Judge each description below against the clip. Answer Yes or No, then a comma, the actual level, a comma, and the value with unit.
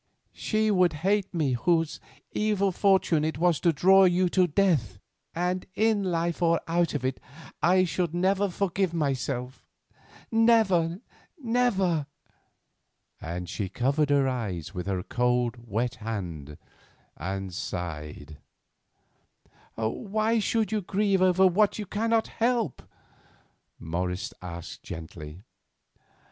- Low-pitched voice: No, medium, 165 Hz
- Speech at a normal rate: No, slow, 115 wpm